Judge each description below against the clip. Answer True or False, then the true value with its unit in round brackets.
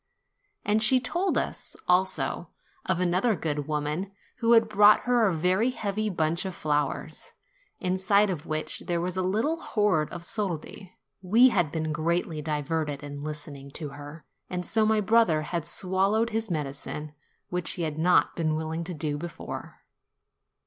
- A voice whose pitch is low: False (175 Hz)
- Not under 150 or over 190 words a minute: True (160 wpm)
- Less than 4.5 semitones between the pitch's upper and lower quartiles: False (5.1 semitones)